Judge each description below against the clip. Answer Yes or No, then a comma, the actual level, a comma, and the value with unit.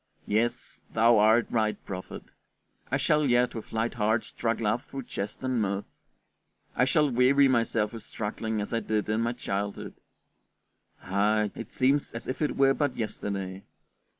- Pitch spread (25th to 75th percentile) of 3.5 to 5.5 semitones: No, average, 3.0 semitones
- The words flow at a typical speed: Yes, average, 160 wpm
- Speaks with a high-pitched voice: No, low, 115 Hz